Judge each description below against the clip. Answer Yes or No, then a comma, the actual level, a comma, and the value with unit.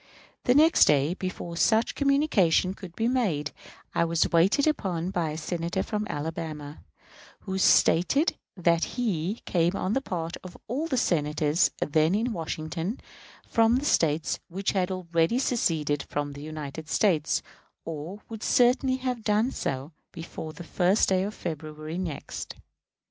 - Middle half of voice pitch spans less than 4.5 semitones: No, wide, 5.6 semitones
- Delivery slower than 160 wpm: Yes, average, 150 wpm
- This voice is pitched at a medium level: Yes, medium, 175 Hz